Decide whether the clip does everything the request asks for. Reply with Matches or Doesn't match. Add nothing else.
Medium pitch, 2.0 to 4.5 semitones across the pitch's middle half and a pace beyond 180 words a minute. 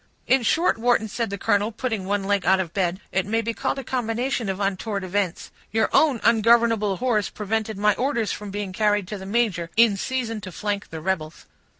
Doesn't match